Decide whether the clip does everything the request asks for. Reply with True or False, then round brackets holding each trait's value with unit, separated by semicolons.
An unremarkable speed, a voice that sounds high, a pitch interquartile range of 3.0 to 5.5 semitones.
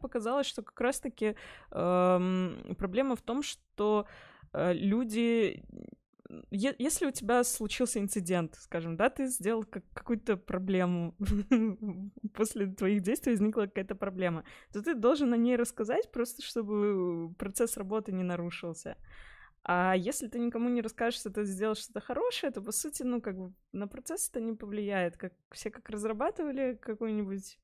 True (150 wpm; 215 Hz; 3.8 semitones)